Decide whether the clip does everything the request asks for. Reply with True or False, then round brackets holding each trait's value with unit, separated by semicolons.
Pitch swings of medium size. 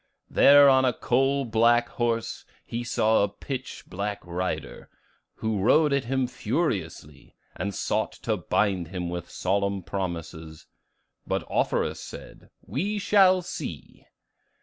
False (6.3 semitones)